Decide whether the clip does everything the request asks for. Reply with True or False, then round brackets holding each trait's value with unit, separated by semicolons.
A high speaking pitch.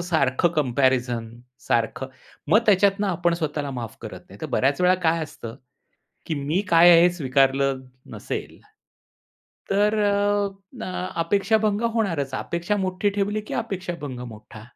False (165 Hz)